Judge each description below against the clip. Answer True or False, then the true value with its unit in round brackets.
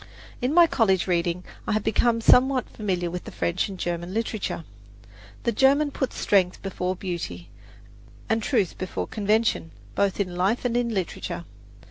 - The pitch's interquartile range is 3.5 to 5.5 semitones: True (4.5 semitones)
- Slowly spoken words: False (150 wpm)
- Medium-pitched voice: False (200 Hz)